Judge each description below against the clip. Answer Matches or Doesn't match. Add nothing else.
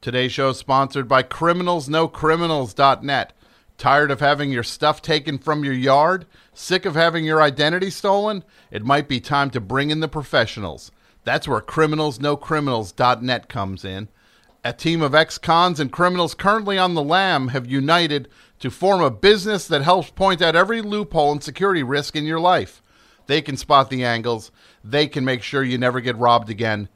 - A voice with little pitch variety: Doesn't match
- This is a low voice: Doesn't match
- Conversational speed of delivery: Matches